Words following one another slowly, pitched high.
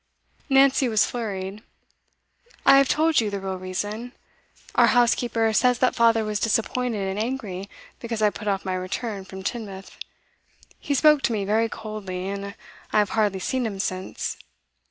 No: average, 160 wpm; high, 215 Hz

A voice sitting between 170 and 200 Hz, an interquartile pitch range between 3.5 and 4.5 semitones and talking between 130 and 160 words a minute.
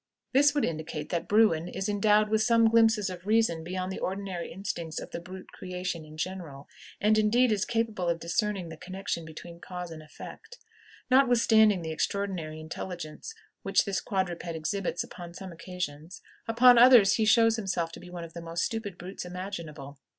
No: medium, 185 Hz; average, 4.2 semitones; average, 175 wpm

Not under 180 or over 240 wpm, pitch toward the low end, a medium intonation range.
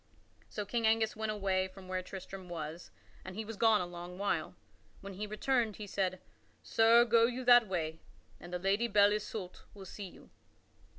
No: average, 190 wpm; high, 200 Hz; average, 3.1 semitones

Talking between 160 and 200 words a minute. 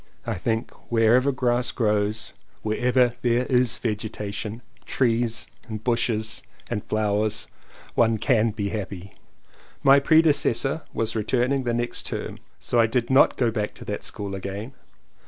No: average, 145 wpm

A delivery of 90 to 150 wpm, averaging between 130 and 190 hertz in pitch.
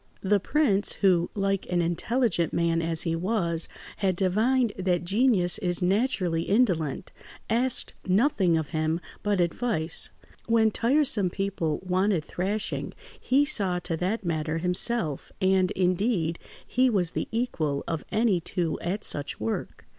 Yes: average, 140 wpm; medium, 185 Hz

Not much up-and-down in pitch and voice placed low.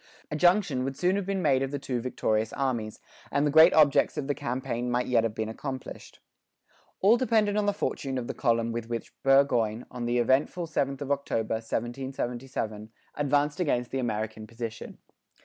No: average, 3.9 semitones; low, 130 Hz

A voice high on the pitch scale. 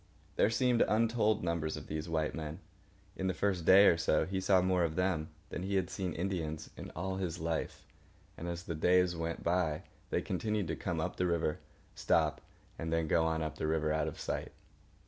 No: very low, 85 Hz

